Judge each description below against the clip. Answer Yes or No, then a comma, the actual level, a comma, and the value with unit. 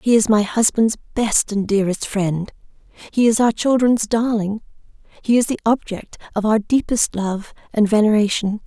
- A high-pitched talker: Yes, high, 215 Hz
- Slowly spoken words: No, average, 160 wpm